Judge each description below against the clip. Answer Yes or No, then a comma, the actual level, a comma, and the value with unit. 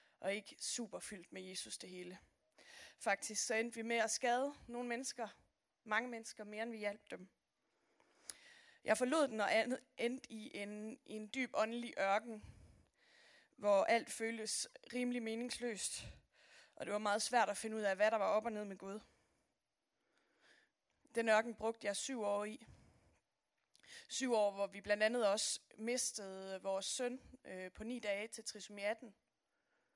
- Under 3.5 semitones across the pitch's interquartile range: Yes, average, 2.8 semitones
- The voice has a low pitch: No, high, 220 Hz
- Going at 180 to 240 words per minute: No, average, 165 wpm